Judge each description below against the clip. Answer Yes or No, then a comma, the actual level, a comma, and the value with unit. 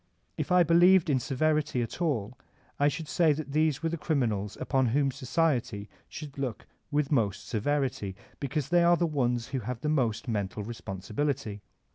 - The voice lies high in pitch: No, medium, 140 Hz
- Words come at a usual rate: Yes, average, 165 wpm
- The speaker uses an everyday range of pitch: Yes, average, 5.0 semitones